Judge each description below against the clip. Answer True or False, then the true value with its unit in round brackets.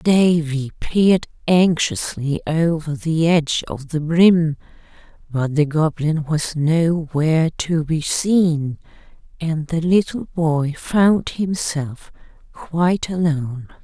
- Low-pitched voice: False (160 Hz)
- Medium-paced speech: False (110 wpm)